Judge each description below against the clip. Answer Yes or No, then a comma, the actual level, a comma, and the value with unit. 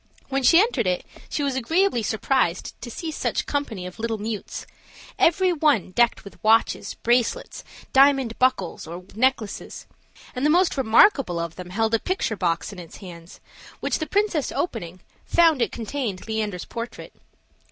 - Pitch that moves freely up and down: Yes, wide, 6.6 semitones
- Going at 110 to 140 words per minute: No, average, 160 wpm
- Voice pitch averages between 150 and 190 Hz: No, high, 230 Hz